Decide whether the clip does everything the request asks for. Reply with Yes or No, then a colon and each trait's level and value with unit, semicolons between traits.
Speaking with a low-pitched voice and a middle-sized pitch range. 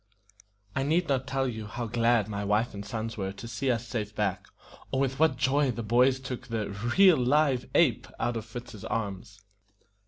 Yes: low, 120 Hz; average, 3.7 semitones